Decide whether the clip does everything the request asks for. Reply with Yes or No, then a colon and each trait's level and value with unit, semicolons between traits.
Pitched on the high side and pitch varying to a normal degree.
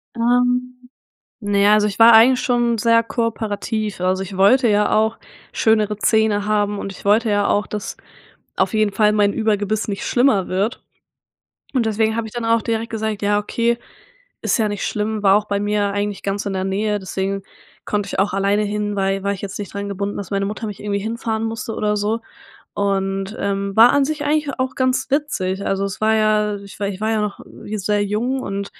No: high, 210 Hz; narrow, 2.0 semitones